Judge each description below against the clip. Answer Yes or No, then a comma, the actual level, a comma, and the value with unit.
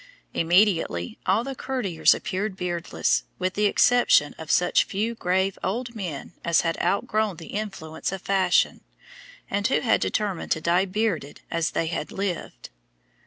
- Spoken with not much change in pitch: No, average, 4.0 semitones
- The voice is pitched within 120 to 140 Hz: No, high, 190 Hz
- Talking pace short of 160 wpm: Yes, average, 150 wpm